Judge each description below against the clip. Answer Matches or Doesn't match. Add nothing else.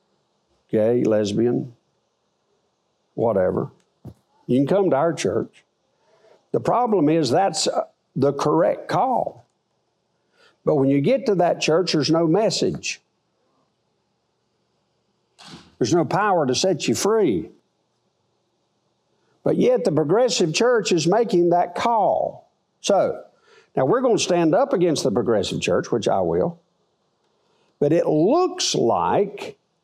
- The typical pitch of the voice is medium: Matches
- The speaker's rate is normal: Doesn't match